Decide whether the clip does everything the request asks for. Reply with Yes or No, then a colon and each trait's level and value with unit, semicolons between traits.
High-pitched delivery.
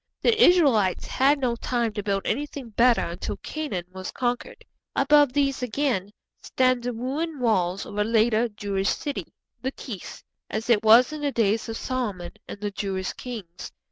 Yes: high, 235 Hz